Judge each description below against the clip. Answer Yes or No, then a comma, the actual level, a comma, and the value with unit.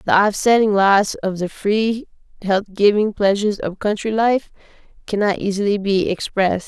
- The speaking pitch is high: Yes, high, 205 Hz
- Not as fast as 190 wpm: Yes, average, 145 wpm